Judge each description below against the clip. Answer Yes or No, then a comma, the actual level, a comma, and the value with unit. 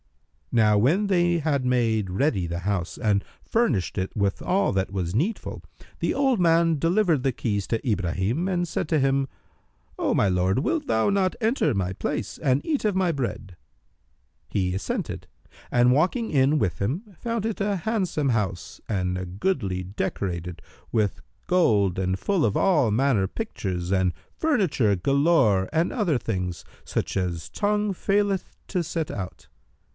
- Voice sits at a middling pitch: No, low, 130 Hz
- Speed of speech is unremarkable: Yes, average, 160 wpm